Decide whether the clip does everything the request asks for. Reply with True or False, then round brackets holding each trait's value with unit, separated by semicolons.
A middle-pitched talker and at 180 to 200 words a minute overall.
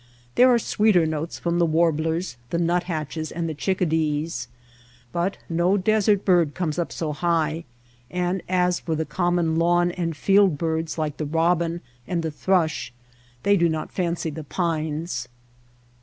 False (170 Hz; 155 wpm)